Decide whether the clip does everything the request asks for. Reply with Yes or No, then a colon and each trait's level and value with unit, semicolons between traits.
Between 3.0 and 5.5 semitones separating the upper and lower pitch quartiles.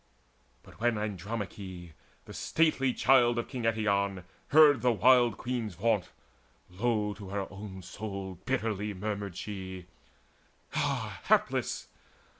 Yes: average, 3.7 semitones